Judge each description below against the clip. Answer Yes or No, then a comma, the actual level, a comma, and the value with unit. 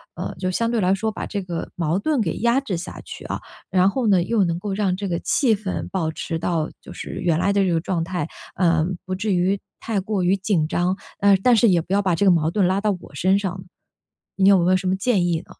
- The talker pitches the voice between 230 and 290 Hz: No, high, 190 Hz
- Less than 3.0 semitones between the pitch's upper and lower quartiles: Yes, narrow, 2.5 semitones